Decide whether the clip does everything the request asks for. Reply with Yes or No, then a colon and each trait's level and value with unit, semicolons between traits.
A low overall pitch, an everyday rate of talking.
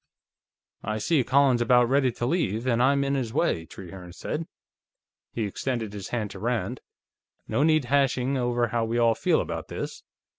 Yes: low, 120 Hz; average, 175 wpm